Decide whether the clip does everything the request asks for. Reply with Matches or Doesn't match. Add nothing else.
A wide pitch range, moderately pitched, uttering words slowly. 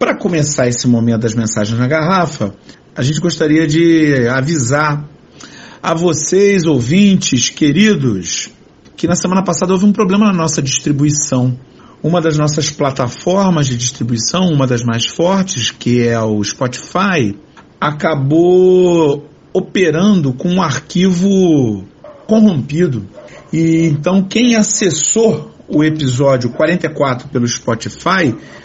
Matches